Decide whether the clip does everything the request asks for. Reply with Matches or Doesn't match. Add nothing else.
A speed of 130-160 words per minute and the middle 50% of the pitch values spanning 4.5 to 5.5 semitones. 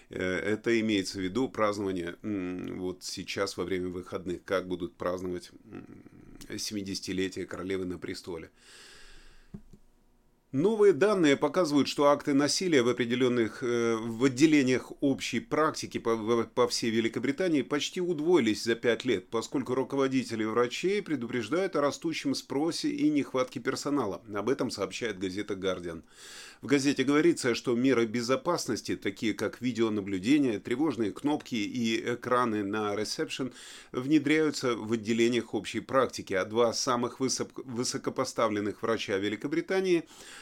Doesn't match